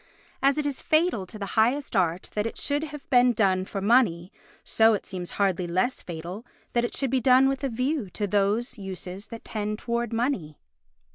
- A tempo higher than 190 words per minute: Yes, average, 200 wpm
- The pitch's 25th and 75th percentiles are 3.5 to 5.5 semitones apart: Yes, average, 5.2 semitones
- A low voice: No, high, 220 Hz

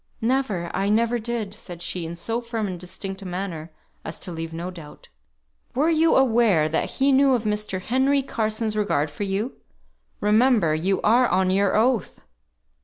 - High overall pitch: Yes, high, 210 Hz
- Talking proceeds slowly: No, average, 175 wpm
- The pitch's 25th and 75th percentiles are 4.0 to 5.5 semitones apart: Yes, average, 4.8 semitones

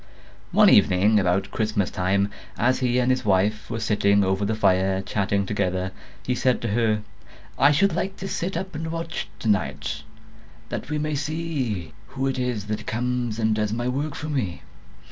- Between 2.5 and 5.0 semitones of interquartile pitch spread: No, wide, 5.4 semitones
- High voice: No, low, 110 Hz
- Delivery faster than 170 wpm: Yes, average, 180 wpm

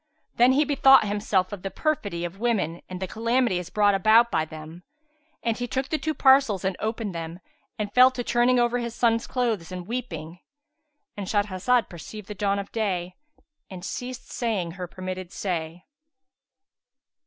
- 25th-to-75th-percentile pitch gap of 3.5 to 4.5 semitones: No, average, 5.1 semitones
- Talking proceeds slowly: No, average, 165 wpm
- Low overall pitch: No, high, 210 Hz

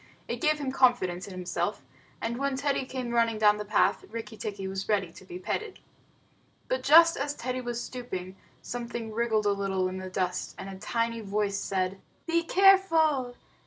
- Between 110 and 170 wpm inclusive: No, average, 180 wpm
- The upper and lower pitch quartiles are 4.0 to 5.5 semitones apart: Yes, average, 5.2 semitones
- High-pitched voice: Yes, high, 230 Hz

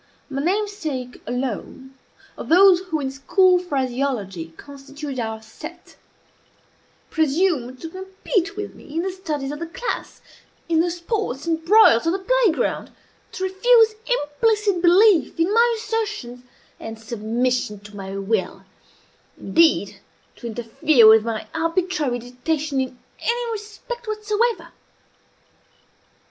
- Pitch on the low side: No, very high, 320 Hz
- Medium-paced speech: No, slow, 125 wpm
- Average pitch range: No, wide, 7.6 semitones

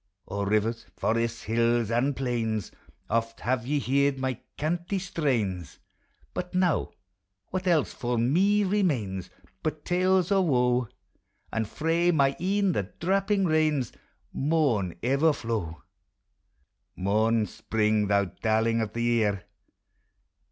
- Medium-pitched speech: No, low, 125 Hz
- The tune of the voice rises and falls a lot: Yes, wide, 6.7 semitones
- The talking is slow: Yes, slow, 120 wpm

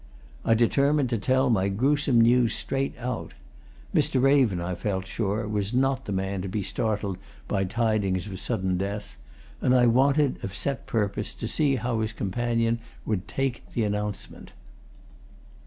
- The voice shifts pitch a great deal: No, average, 4.2 semitones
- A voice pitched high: No, low, 110 Hz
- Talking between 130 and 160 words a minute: Yes, average, 155 wpm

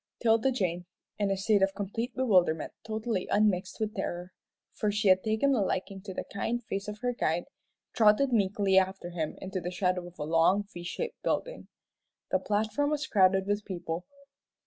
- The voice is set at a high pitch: Yes, high, 200 Hz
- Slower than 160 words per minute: No, average, 180 wpm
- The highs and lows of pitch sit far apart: No, average, 3.1 semitones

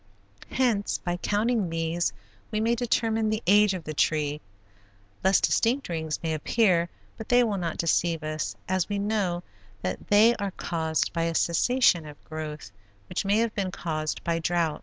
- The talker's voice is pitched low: No, medium, 175 Hz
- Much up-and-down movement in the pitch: No, average, 5.0 semitones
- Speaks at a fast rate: No, average, 170 wpm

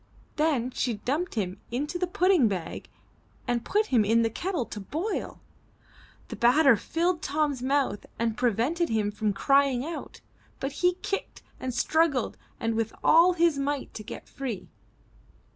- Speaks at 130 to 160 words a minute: Yes, average, 155 wpm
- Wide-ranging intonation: Yes, wide, 6.2 semitones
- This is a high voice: Yes, very high, 270 Hz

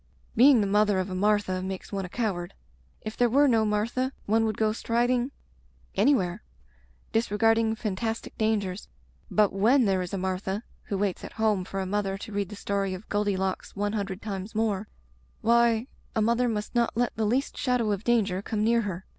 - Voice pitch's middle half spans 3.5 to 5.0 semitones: No, average, 2.7 semitones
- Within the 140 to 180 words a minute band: No, average, 190 wpm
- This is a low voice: No, high, 210 Hz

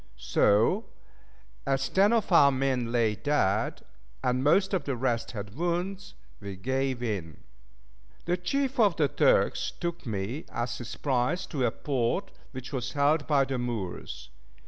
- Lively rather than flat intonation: Yes, wide, 6.4 semitones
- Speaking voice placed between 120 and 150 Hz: Yes, low, 135 Hz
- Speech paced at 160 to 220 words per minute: No, average, 150 wpm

